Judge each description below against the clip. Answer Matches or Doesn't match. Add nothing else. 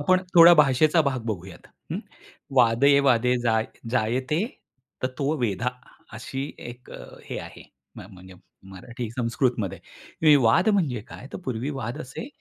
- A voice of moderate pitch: Doesn't match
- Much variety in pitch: Doesn't match